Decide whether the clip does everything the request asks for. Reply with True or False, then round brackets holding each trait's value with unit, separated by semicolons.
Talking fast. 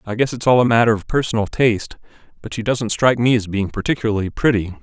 True (225 wpm)